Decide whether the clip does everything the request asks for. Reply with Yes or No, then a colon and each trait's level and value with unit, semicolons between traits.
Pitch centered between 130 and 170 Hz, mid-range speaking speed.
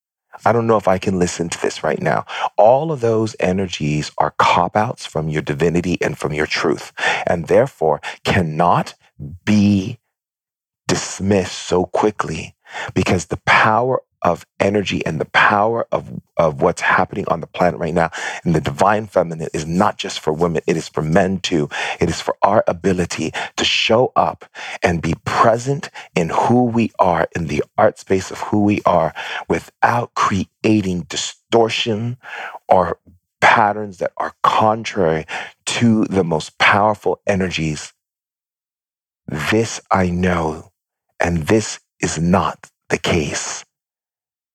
No: very low, 95 Hz; average, 145 wpm